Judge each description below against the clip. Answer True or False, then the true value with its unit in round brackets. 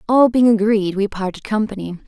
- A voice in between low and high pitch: False (210 Hz)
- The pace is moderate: True (175 wpm)